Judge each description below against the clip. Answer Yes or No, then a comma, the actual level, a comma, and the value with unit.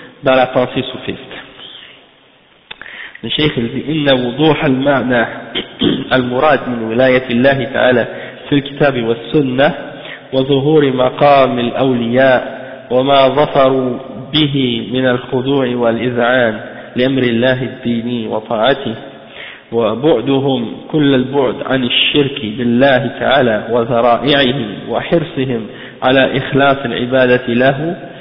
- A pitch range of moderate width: No, narrow, 2.1 semitones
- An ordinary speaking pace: No, slow, 85 wpm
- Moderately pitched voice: No, low, 130 Hz